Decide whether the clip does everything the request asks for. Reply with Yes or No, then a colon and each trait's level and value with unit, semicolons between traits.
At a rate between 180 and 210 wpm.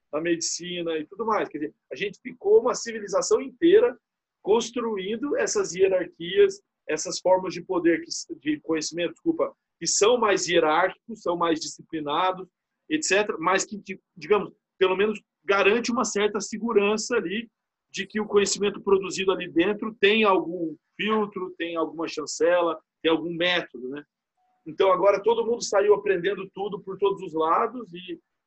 No: average, 150 wpm